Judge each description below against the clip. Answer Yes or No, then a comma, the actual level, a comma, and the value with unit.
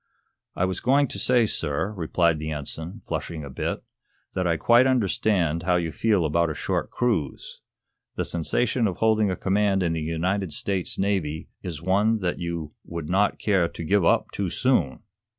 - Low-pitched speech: Yes, very low, 90 Hz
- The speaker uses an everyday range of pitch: Yes, average, 4.0 semitones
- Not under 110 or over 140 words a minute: No, average, 180 wpm